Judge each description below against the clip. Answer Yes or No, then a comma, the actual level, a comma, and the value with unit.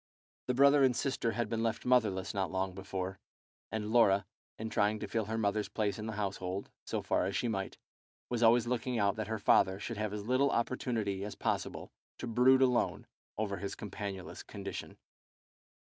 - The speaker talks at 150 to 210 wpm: Yes, average, 185 wpm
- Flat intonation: No, average, 3.1 semitones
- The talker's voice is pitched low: Yes, low, 110 Hz